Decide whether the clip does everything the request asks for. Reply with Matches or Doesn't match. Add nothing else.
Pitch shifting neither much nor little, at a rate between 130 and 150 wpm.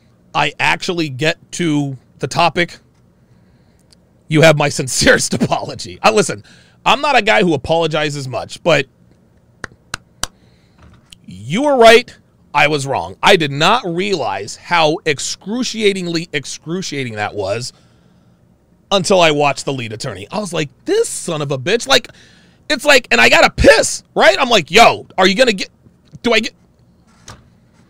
Doesn't match